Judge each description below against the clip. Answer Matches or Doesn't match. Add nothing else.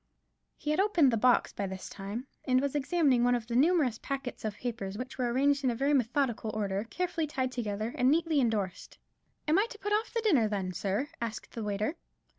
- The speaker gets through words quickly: Matches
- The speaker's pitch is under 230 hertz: Doesn't match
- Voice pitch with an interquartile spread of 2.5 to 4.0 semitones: Doesn't match